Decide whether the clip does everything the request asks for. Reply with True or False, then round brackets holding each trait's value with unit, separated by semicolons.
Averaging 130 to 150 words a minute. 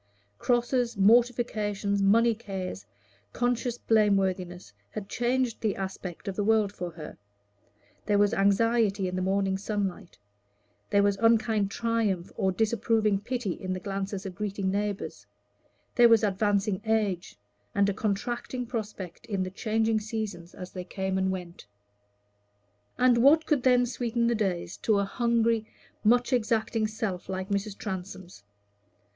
True (140 wpm)